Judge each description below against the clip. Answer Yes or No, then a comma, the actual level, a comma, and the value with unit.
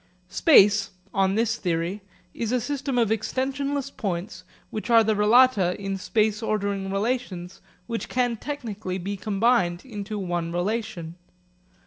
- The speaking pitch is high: Yes, high, 210 Hz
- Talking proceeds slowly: Yes, slow, 130 wpm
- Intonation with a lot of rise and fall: No, average, 3.9 semitones